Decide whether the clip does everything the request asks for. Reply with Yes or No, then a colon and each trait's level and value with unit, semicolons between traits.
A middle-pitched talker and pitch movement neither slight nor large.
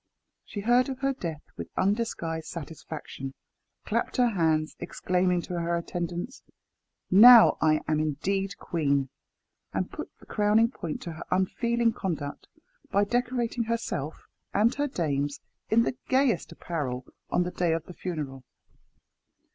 No: medium, 180 Hz; wide, 6.7 semitones